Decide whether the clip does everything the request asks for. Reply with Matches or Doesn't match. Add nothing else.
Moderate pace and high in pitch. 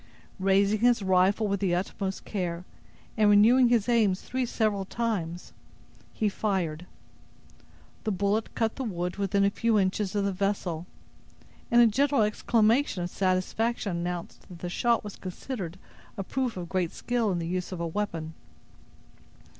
Matches